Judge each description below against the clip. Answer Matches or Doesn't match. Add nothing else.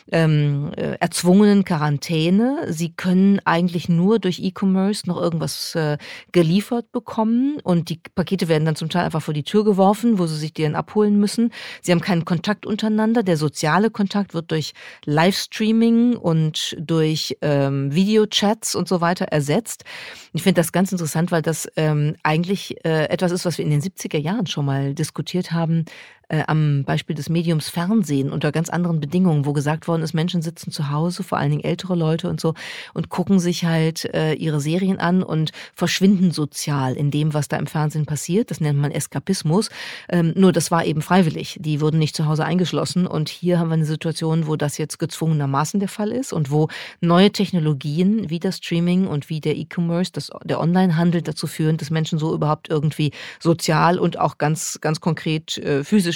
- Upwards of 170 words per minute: Matches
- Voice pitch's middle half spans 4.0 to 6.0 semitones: Doesn't match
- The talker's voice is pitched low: Doesn't match